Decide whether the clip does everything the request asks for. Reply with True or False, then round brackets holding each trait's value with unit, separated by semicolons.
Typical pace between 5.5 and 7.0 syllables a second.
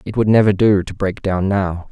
False (5.0 syllables/s)